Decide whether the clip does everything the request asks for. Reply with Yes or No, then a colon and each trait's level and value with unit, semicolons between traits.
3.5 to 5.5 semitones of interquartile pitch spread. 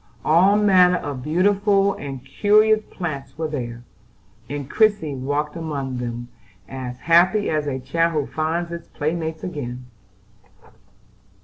Yes: average, 5.1 semitones